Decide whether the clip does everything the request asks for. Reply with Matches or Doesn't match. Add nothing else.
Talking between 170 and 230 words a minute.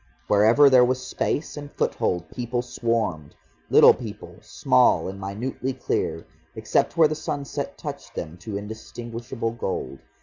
Doesn't match